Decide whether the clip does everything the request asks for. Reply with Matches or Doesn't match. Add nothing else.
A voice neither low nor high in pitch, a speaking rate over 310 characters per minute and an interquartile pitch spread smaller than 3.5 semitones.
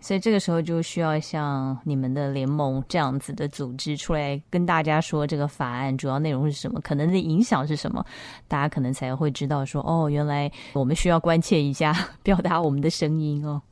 Matches